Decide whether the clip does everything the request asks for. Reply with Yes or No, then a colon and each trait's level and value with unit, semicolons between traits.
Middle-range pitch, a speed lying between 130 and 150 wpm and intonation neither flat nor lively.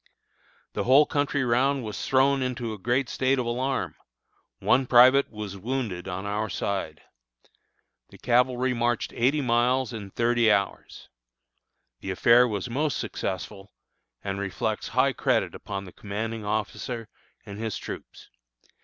No: low, 120 Hz; slow, 135 wpm; average, 3.9 semitones